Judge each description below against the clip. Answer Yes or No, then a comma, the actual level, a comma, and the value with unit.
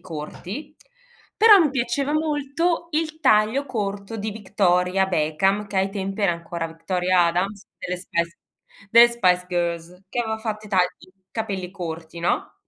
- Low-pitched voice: No, high, 195 Hz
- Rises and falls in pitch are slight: No, average, 4.9 semitones